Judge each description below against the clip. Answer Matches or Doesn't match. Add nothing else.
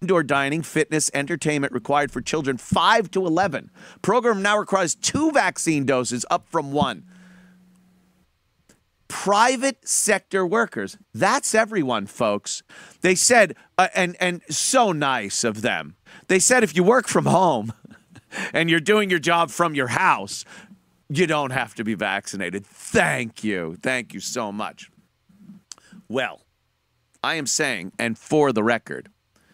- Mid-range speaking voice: Matches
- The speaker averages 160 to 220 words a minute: Doesn't match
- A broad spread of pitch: Matches